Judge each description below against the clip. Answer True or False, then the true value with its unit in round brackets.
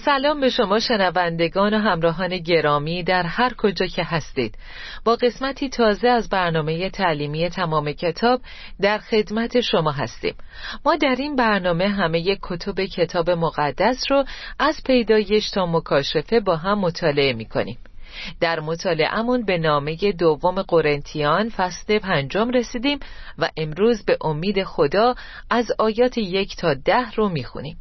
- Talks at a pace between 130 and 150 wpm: True (135 wpm)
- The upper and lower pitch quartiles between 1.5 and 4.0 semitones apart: False (5.5 semitones)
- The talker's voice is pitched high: True (195 Hz)